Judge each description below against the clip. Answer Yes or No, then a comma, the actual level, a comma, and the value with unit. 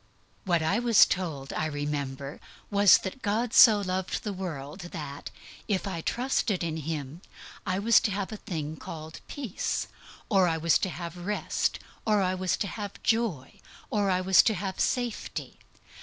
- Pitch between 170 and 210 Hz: Yes, medium, 185 Hz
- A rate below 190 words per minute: Yes, average, 170 wpm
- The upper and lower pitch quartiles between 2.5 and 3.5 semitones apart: No, average, 4.5 semitones